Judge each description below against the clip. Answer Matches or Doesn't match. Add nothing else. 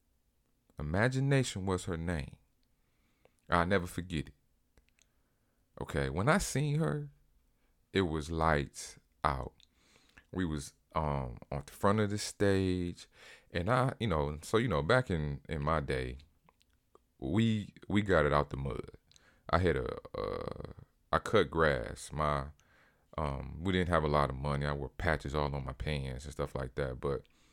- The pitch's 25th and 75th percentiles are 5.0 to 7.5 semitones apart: Matches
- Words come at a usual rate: Matches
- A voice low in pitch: Matches